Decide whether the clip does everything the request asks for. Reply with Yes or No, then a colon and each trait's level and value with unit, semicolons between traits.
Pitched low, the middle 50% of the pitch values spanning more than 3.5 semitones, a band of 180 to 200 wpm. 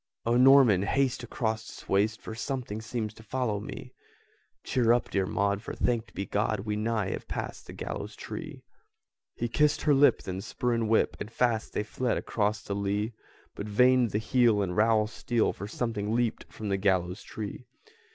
No: low, 110 Hz; average, 2.8 semitones; average, 185 wpm